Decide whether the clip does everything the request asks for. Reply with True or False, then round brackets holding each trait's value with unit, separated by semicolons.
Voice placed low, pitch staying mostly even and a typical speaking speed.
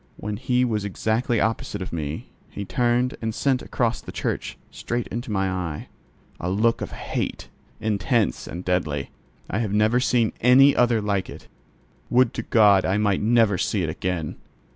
False (105 Hz; 4.1 semitones; 170 wpm)